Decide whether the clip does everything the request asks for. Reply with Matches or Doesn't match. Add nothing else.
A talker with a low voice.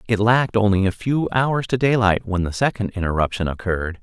Matches